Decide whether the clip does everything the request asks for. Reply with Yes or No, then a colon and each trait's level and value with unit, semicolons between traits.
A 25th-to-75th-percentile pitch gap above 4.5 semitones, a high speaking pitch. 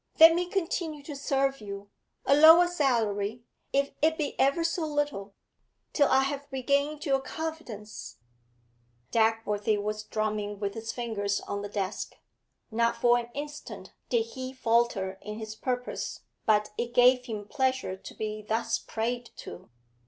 Yes: average, 5.0 semitones; high, 235 Hz